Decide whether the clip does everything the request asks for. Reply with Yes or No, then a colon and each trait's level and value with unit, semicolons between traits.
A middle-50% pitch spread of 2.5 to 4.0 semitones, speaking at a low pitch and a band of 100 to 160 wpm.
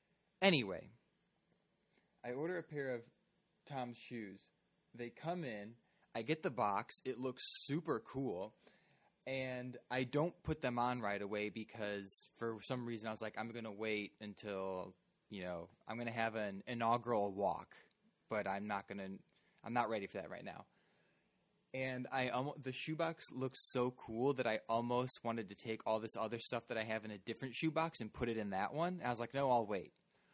No: average, 3.4 semitones; low, 120 Hz; average, 190 wpm